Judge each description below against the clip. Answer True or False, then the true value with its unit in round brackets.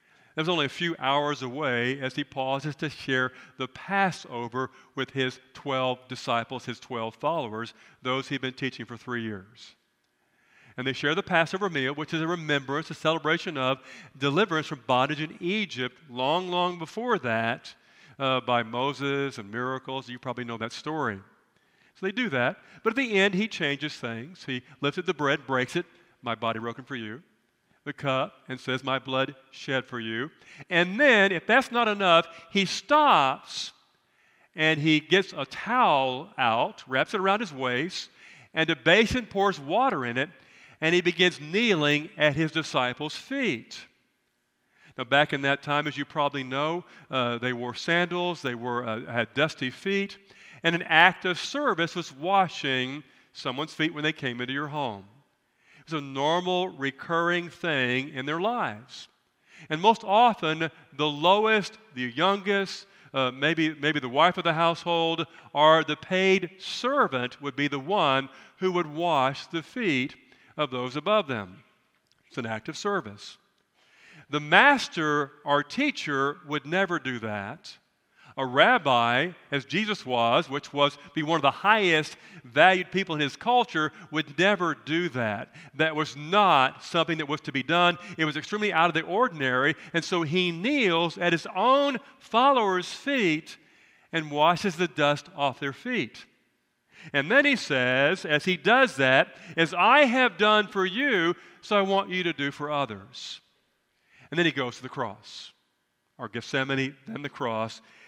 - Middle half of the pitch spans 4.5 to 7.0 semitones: True (5.3 semitones)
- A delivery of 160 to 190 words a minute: True (165 wpm)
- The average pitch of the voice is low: False (150 Hz)